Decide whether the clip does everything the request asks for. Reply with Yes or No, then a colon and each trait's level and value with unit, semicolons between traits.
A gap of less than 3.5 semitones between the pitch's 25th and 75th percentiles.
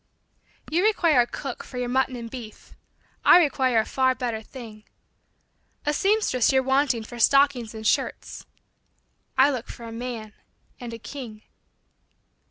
Yes: average, 3.1 semitones